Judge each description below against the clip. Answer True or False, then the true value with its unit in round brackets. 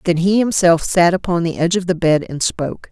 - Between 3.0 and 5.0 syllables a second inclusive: False (5.8 syllables/s)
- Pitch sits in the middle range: True (175 Hz)